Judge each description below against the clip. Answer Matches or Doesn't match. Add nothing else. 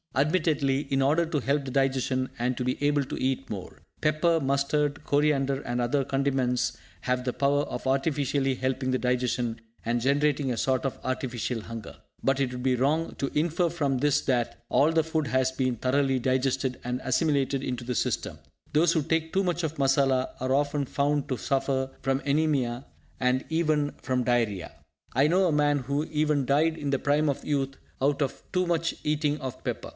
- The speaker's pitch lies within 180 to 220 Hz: Doesn't match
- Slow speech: Doesn't match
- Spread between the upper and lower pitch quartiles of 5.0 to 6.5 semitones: Doesn't match